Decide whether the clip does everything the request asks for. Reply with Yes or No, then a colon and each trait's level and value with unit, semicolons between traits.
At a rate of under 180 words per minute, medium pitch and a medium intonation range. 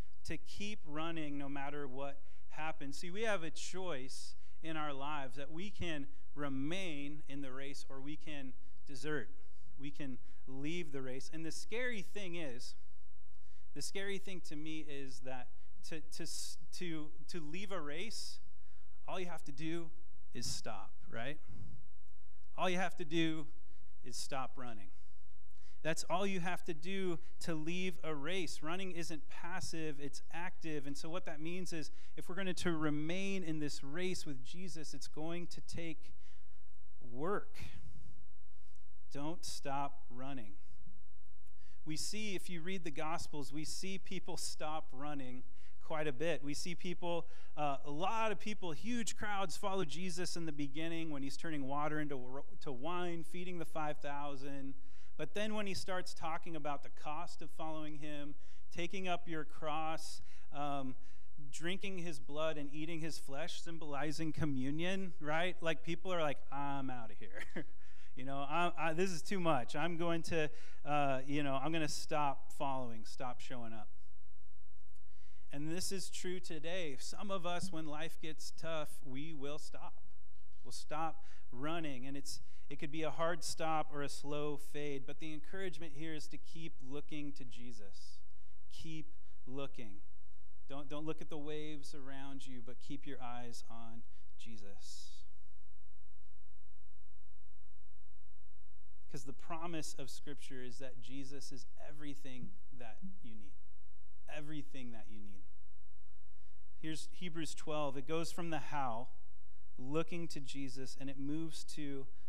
No: average, 155 wpm; medium, 145 Hz; wide, 7.6 semitones